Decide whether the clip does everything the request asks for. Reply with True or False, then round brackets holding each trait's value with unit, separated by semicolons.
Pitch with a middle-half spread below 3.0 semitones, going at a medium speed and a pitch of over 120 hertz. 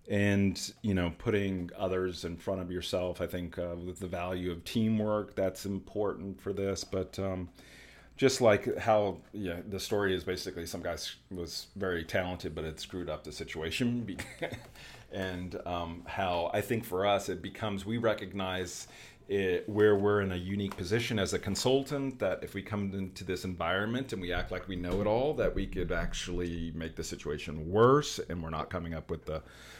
False (2.6 semitones; 185 wpm; 95 Hz)